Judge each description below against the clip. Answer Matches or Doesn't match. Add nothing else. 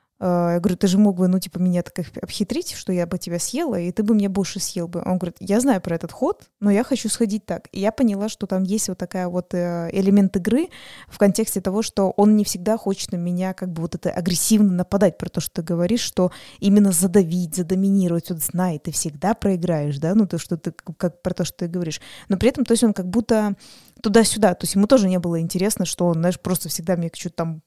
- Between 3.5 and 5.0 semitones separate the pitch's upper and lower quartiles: Doesn't match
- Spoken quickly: Matches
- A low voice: Doesn't match